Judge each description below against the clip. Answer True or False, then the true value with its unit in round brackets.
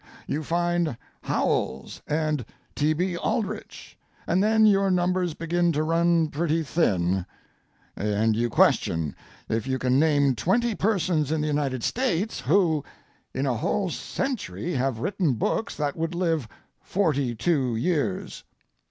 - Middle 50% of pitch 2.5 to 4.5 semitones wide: False (5.2 semitones)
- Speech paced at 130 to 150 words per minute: True (135 wpm)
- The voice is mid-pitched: True (160 Hz)